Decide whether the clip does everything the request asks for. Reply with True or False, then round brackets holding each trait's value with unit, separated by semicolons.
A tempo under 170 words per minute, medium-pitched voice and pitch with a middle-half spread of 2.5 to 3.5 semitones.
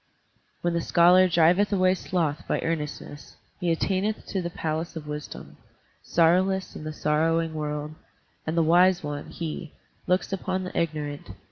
True (150 wpm; 165 Hz; 3.1 semitones)